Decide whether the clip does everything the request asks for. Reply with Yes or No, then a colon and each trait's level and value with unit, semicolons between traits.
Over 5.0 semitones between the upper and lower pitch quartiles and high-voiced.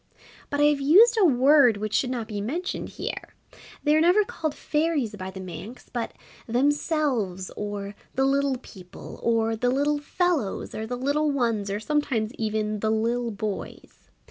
Yes: wide, 5.5 semitones; high, 245 Hz